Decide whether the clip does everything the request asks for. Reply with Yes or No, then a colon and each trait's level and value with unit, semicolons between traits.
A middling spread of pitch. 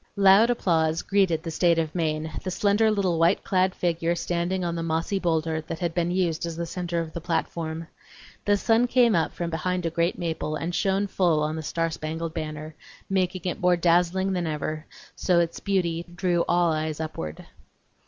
No: narrow, 2.3 semitones